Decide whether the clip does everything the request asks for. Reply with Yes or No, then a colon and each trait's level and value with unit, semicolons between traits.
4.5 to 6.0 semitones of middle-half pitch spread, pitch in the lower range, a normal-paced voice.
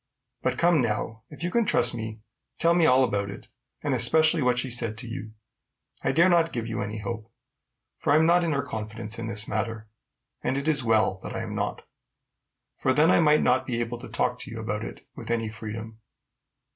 No: average, 5.2 semitones; low, 120 Hz; fast, 220 wpm